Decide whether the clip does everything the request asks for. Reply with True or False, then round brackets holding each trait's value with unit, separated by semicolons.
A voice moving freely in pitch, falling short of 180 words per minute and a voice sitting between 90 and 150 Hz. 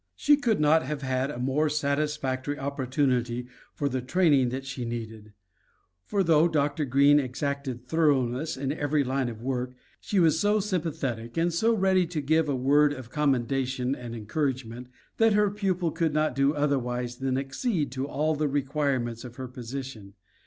False (3.3 semitones; 165 wpm; 140 Hz)